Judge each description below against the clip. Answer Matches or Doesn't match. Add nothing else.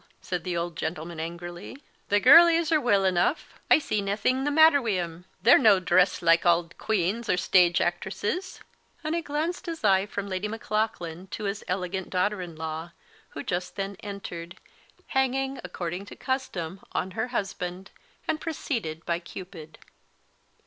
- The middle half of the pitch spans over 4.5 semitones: Matches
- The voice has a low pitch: Doesn't match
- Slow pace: Doesn't match